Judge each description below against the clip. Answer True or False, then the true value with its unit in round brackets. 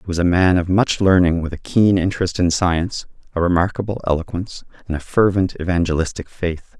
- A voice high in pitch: False (90 Hz)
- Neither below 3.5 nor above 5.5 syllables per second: False (6.2 syllables/s)